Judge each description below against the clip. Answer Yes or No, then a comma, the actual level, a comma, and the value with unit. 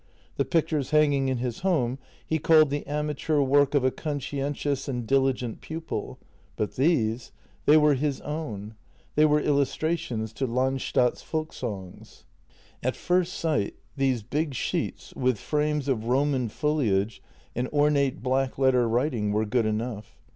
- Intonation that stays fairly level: No, average, 3.7 semitones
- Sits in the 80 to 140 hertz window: Yes, low, 135 Hz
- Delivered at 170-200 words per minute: No, average, 145 wpm